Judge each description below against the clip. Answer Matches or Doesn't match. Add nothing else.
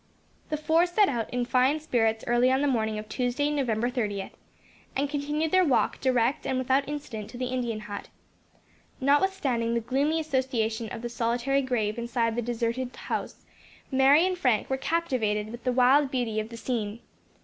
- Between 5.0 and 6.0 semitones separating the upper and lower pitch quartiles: Doesn't match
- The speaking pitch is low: Doesn't match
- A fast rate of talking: Doesn't match